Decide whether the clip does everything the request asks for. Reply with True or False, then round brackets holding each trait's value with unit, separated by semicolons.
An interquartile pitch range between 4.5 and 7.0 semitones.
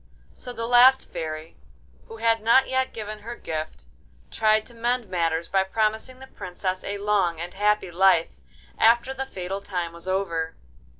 True (4.8 semitones)